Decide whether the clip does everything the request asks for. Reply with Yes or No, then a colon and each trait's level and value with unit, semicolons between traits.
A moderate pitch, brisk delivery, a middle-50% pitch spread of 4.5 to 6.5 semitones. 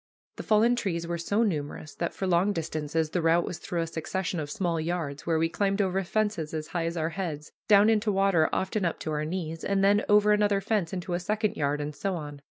No: medium, 175 Hz; fast, 235 wpm; average, 3.8 semitones